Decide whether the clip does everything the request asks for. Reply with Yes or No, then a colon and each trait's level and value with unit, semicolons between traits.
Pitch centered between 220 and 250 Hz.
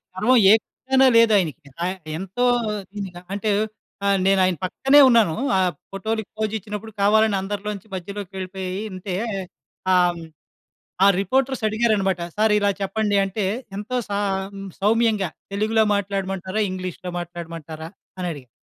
No: high, 200 Hz